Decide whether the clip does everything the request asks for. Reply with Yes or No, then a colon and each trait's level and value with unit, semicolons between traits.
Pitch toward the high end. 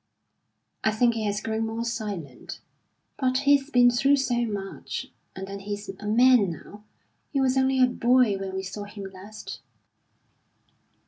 Yes: high, 220 Hz